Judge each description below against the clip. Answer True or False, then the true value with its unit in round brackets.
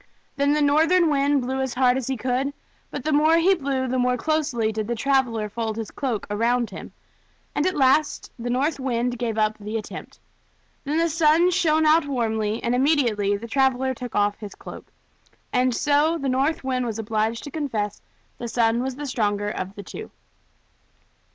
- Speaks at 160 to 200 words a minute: True (190 wpm)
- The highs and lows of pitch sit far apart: False (4.2 semitones)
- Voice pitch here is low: False (255 Hz)